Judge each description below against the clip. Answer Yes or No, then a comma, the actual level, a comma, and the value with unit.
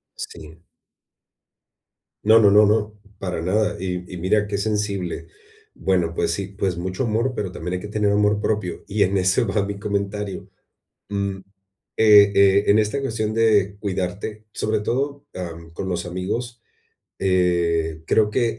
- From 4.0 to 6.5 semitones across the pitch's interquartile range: No, average, 2.7 semitones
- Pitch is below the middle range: Yes, low, 100 Hz